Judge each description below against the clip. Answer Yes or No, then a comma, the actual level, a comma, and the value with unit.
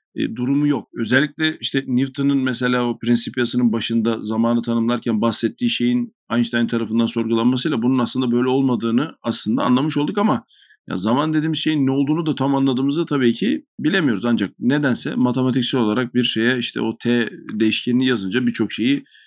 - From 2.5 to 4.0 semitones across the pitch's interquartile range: Yes, average, 3.7 semitones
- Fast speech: Yes, fast, 155 wpm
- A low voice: Yes, low, 125 Hz